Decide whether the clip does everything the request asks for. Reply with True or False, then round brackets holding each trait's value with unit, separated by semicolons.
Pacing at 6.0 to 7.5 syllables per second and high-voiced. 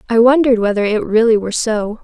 True (6.5 syllables/s; 225 Hz)